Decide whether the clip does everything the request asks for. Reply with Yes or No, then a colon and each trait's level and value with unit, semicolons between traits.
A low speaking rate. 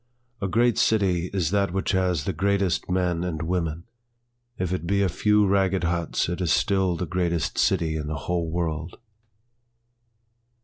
No: average, 165 wpm